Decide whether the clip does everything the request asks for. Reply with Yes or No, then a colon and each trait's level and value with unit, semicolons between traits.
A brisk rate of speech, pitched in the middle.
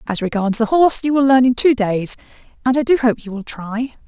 No: fast, 250 wpm; high, 240 Hz